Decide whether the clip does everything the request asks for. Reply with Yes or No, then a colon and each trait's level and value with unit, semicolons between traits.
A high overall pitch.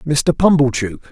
No: medium, 140 Hz